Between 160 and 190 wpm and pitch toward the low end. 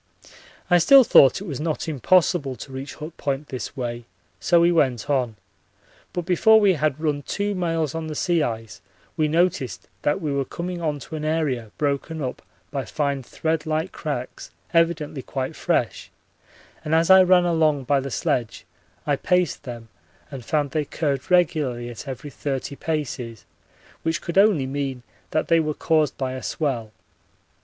No: average, 170 wpm; medium, 150 Hz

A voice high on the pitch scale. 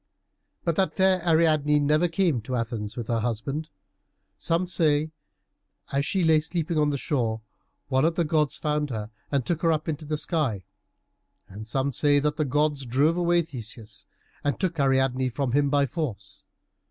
No: medium, 145 Hz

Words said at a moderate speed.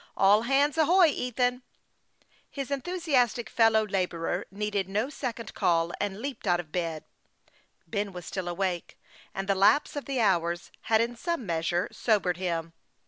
Yes: average, 160 wpm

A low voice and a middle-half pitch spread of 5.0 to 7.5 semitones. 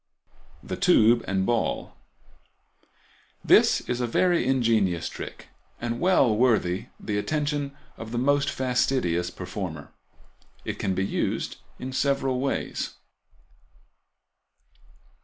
Yes: low, 120 Hz; wide, 5.5 semitones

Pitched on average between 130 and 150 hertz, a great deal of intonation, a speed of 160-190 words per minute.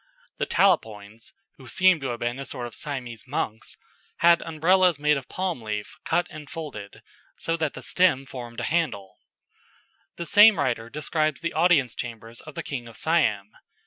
Yes: medium, 140 Hz; wide, 6.1 semitones; average, 175 wpm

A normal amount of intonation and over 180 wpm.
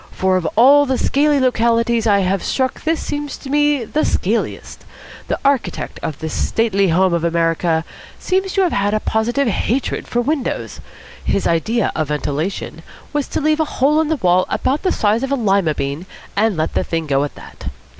No: wide, 8.0 semitones; average, 195 wpm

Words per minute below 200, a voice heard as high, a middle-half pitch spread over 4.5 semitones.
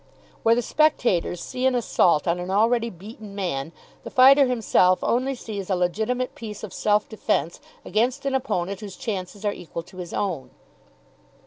Yes: average, 165 wpm; high, 210 Hz; average, 5.2 semitones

